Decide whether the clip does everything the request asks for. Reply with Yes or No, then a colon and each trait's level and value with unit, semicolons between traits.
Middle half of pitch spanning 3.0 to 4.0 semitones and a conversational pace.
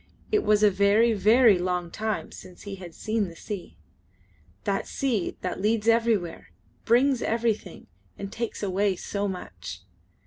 Yes: average, 3.3 semitones; average, 145 wpm